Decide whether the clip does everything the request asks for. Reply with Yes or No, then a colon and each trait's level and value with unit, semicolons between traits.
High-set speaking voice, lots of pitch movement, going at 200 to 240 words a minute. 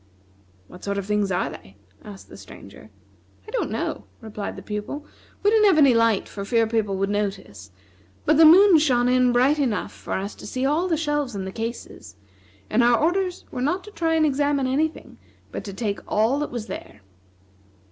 Yes: high, 245 Hz; wide, 6.6 semitones; fast, 205 wpm